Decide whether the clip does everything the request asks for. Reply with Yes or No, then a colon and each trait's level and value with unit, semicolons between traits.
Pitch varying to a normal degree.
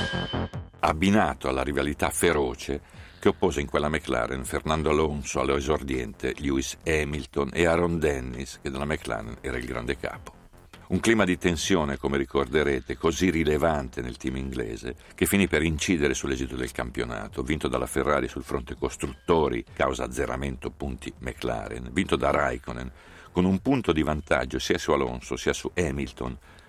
Yes: average, 4.4 semitones